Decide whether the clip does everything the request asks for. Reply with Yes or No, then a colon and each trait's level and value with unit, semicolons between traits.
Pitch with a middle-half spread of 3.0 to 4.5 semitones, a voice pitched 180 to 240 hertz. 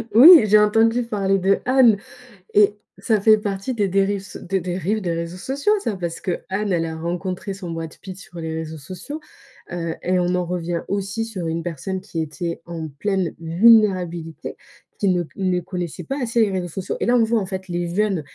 Yes: average, 3.5 semitones; medium, 185 Hz